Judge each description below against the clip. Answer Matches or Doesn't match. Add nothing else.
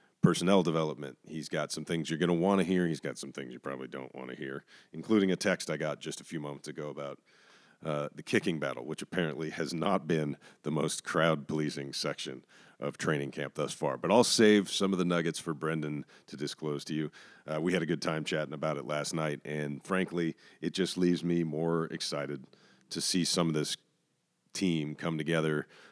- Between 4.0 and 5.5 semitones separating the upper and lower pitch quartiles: Doesn't match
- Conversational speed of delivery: Doesn't match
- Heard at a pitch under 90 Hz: Matches